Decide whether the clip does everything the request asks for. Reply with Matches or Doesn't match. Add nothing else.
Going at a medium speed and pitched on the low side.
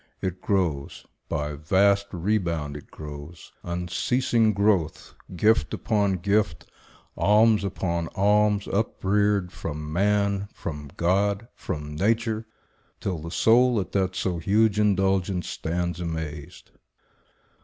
Doesn't match